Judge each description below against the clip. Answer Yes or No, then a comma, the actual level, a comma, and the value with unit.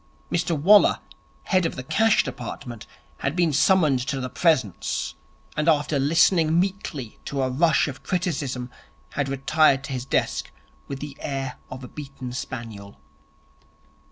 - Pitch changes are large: No, average, 4.2 semitones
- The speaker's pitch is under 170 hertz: Yes, medium, 140 Hz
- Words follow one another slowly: No, average, 145 wpm